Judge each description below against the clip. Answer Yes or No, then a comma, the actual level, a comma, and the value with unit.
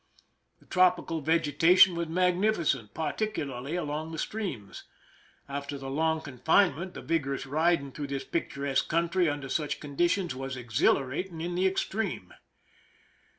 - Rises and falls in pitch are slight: No, average, 4.0 semitones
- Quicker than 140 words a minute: No, slow, 135 wpm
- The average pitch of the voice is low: No, medium, 160 Hz